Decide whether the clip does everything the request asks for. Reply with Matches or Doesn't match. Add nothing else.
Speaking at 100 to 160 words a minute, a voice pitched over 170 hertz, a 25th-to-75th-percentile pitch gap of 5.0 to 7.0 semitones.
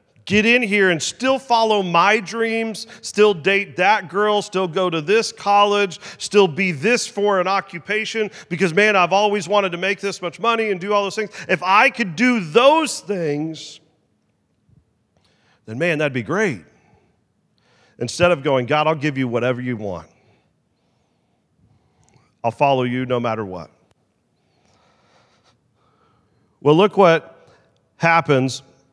Matches